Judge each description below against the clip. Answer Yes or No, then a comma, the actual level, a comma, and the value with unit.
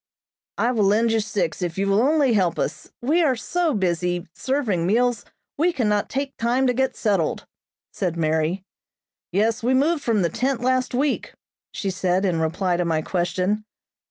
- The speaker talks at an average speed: Yes, average, 170 wpm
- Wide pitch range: Yes, wide, 6.1 semitones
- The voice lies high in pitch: Yes, high, 215 Hz